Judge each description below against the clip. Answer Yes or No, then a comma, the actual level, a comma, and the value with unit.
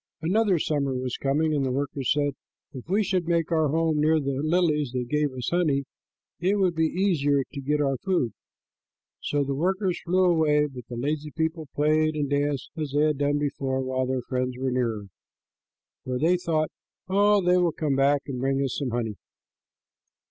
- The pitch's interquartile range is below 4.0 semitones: Yes, average, 3.5 semitones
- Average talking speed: Yes, average, 190 wpm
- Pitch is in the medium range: Yes, medium, 150 Hz